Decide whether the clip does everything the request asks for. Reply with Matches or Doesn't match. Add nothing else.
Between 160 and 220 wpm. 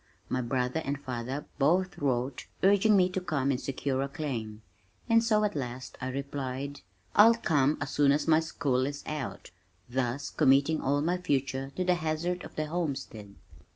Matches